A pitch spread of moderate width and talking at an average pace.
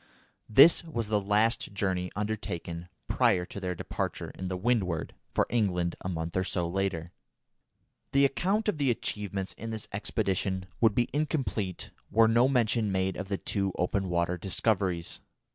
Yes: average, 3.8 semitones; average, 155 wpm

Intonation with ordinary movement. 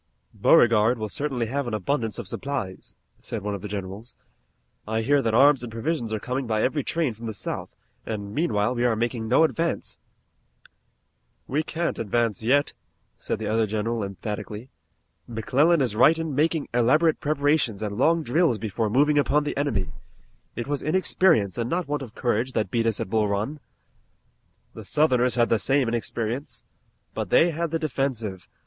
Yes: average, 5.0 semitones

